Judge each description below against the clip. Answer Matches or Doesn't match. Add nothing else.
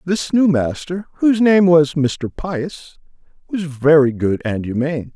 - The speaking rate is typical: Matches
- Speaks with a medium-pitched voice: Matches